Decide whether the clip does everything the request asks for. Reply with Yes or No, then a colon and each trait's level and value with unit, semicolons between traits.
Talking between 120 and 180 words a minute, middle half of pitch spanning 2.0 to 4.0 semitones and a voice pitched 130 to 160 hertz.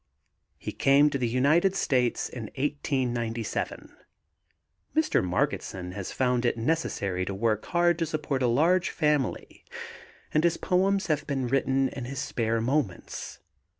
No: average, 140 wpm; average, 4.7 semitones; low, 135 Hz